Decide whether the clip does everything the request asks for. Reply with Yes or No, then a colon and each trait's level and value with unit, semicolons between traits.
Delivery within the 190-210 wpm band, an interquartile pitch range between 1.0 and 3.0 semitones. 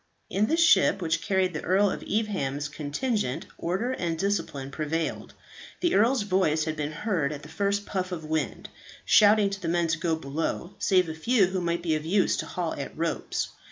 No: average, 195 wpm; average, 4.2 semitones